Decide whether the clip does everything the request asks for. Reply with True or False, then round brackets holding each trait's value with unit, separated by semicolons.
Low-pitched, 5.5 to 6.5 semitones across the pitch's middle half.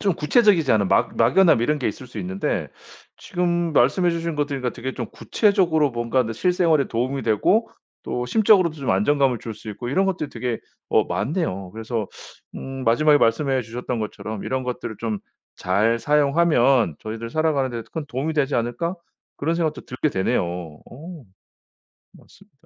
True (130 Hz; 5.8 semitones)